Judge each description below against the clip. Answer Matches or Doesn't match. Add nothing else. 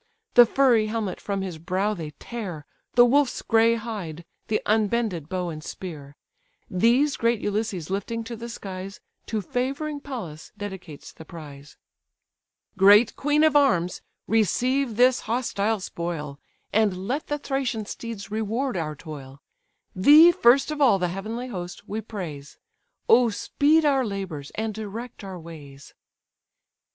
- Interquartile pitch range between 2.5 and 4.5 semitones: Doesn't match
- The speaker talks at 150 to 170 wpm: Doesn't match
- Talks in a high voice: Matches